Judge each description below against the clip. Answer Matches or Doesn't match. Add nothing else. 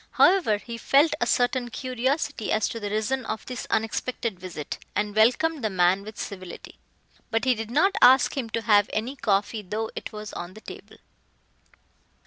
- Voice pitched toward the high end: Matches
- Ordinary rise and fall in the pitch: Matches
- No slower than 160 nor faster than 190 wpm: Matches